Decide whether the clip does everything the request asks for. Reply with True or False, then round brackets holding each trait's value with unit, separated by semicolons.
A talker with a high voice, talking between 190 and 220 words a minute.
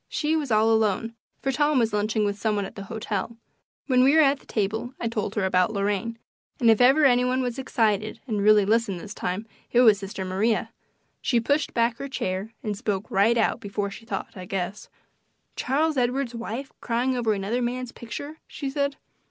True (225 Hz; 200 wpm)